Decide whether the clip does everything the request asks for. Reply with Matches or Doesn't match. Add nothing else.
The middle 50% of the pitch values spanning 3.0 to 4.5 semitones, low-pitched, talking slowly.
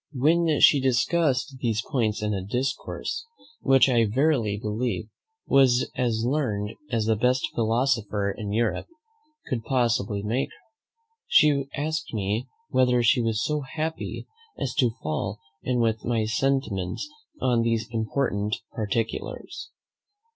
Matches